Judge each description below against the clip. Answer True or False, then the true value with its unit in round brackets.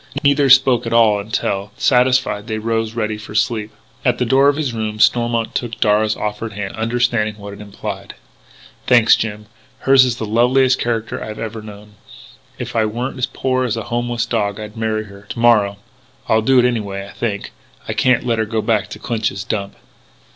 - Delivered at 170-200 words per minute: True (195 wpm)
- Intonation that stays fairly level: True (2.3 semitones)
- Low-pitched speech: True (110 Hz)